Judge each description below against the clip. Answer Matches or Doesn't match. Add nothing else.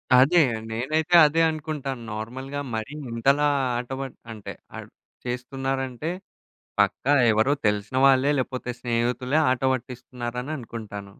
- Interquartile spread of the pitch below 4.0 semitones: Matches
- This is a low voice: Matches